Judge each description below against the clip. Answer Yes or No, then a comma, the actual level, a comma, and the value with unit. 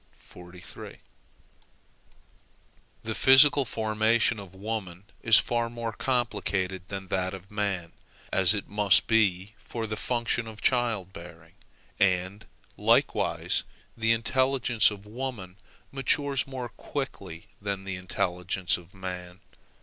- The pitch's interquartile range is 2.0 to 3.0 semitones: No, average, 4.0 semitones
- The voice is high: No, low, 105 Hz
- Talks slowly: Yes, slow, 110 wpm